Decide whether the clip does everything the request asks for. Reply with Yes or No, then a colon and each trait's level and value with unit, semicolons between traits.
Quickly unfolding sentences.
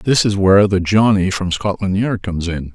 Yes: fast, 220 wpm